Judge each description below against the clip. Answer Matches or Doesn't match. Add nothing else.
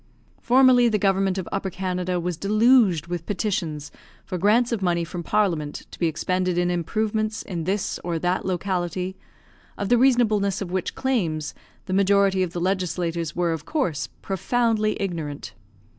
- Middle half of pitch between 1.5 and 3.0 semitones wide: Doesn't match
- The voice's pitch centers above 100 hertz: Matches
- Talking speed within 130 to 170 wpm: Matches